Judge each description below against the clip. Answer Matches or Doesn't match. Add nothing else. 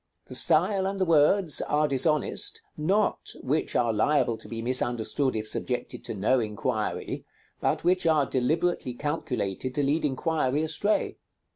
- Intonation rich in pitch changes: Doesn't match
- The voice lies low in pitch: Doesn't match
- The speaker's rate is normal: Matches